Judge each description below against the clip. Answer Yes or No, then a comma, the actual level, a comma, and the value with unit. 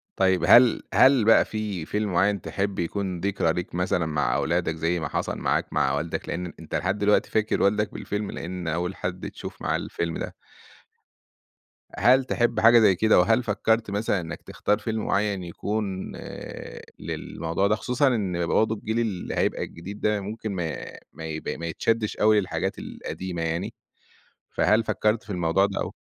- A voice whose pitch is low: Yes, low, 100 Hz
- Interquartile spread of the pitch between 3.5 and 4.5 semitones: Yes, average, 3.8 semitones